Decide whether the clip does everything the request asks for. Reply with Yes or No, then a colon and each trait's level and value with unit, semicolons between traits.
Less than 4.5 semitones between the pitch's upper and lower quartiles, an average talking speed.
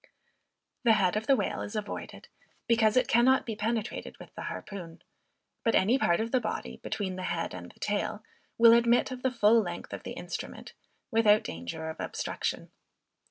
Yes: average, 3.6 semitones; average, 180 wpm